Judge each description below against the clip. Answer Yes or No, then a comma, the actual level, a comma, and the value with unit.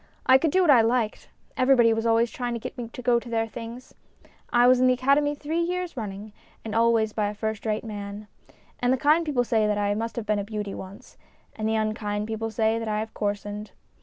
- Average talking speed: No, fast, 240 wpm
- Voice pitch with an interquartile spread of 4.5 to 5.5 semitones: No, average, 2.8 semitones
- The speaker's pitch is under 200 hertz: No, high, 225 Hz